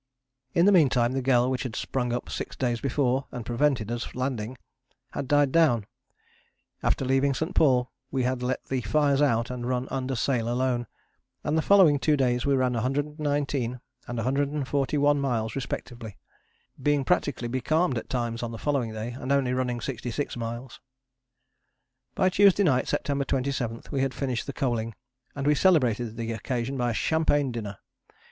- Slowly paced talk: No, average, 165 wpm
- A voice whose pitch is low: Yes, low, 130 Hz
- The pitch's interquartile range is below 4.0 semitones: Yes, average, 2.9 semitones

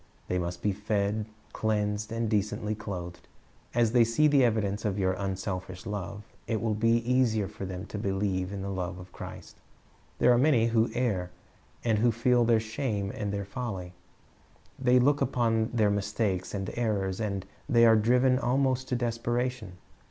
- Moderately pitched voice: No, low, 110 Hz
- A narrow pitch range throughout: No, average, 3.4 semitones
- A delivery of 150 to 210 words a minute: Yes, average, 170 wpm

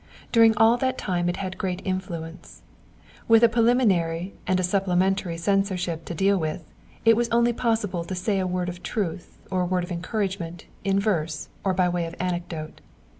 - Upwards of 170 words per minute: Yes, average, 180 wpm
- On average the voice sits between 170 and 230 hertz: Yes, medium, 185 Hz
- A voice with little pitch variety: No, average, 3.1 semitones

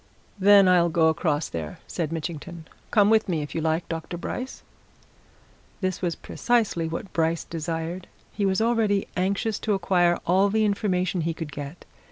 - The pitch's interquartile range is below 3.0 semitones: No, average, 3.5 semitones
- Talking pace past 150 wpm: Yes, average, 165 wpm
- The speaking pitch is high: No, medium, 175 Hz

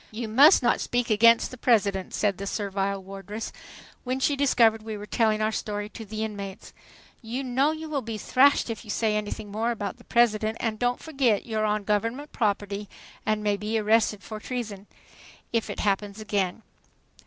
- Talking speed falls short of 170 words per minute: No, average, 185 wpm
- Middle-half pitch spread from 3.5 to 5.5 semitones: No, narrow, 2.5 semitones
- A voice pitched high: Yes, high, 215 Hz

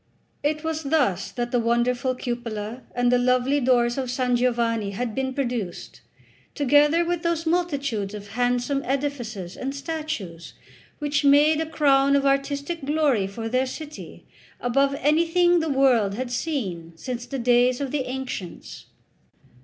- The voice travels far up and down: No, average, 3.4 semitones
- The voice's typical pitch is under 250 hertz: No, very high, 260 Hz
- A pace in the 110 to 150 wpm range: Yes, average, 145 wpm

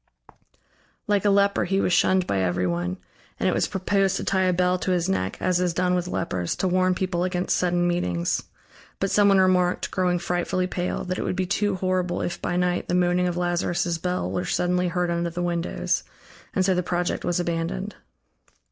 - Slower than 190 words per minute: No, average, 200 wpm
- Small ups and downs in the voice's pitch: Yes, narrow, 1.1 semitones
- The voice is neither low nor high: Yes, medium, 180 Hz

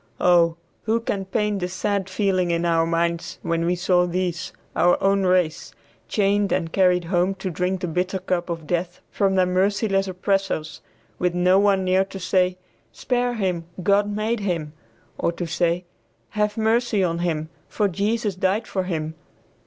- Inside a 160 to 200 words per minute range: Yes, average, 170 wpm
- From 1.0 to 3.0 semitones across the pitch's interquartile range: Yes, narrow, 2.4 semitones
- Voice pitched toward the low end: No, medium, 185 Hz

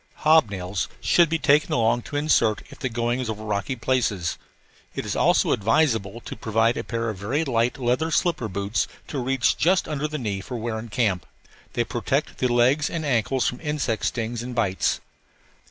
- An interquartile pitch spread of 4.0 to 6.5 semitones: Yes, average, 4.3 semitones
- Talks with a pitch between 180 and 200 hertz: No, low, 120 Hz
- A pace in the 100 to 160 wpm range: No, average, 195 wpm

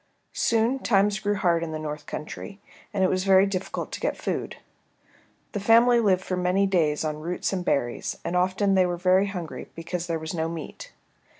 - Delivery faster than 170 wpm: Yes, average, 195 wpm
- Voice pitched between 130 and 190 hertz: Yes, medium, 185 Hz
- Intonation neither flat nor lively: Yes, average, 3.2 semitones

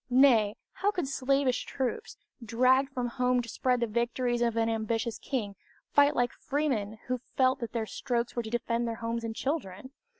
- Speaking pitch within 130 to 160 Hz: No, high, 240 Hz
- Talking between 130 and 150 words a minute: No, average, 180 wpm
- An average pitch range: No, narrow, 2.3 semitones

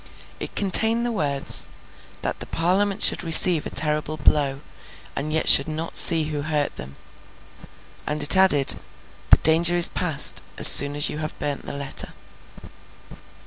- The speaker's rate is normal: Yes, average, 155 wpm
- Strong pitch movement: No, average, 3.2 semitones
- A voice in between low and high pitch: Yes, medium, 155 Hz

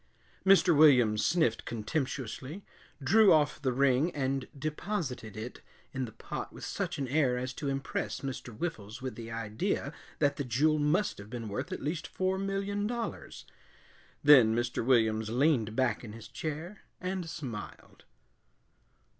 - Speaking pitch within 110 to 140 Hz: Yes, low, 135 Hz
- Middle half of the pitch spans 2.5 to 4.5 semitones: No, wide, 5.4 semitones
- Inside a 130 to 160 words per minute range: Yes, average, 150 wpm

